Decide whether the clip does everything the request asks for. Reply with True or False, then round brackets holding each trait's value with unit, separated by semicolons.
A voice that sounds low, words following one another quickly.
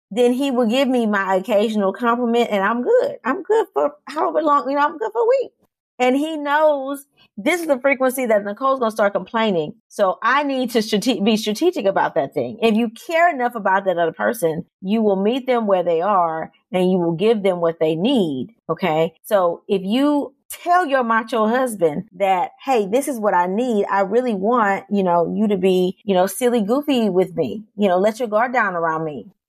False (225 Hz; 215 wpm)